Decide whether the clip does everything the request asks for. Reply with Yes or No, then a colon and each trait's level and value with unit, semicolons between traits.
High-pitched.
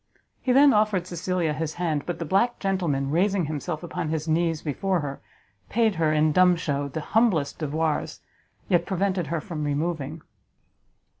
No: medium, 165 Hz